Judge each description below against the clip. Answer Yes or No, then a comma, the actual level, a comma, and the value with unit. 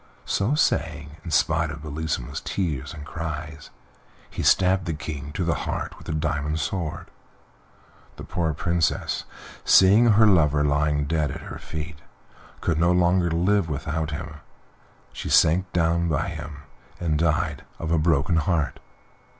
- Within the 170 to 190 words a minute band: No, average, 150 wpm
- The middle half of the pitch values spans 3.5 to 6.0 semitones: No, narrow, 2.5 semitones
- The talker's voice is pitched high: No, very low, 80 Hz